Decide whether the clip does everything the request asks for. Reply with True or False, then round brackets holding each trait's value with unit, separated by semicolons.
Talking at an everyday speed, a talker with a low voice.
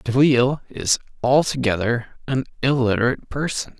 False (95 wpm; 130 Hz)